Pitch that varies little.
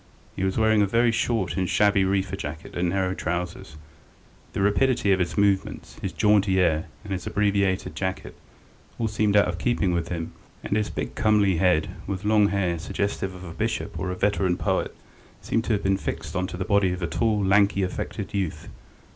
Yes: narrow, 2.3 semitones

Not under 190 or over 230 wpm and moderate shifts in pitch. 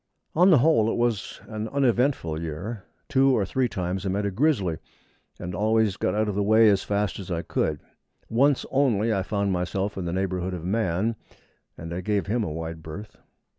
Yes: average, 200 wpm; average, 4.0 semitones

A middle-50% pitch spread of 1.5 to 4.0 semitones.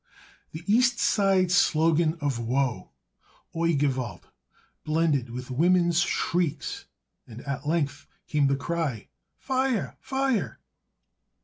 No: average, 4.7 semitones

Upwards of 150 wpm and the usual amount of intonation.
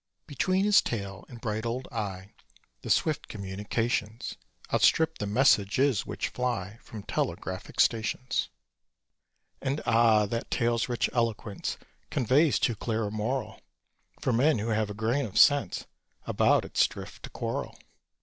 No: average, 140 wpm; average, 3.7 semitones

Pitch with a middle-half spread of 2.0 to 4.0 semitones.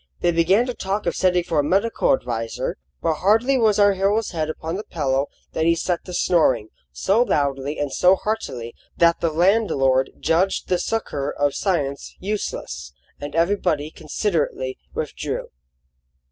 No: wide, 5.5 semitones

